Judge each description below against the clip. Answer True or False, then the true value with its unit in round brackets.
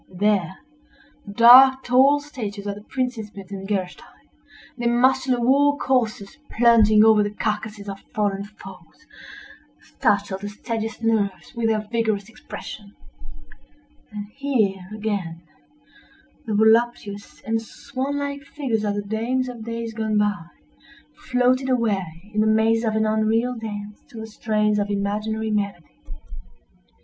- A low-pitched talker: False (220 Hz)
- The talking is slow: True (125 wpm)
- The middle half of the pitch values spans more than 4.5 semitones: False (3.0 semitones)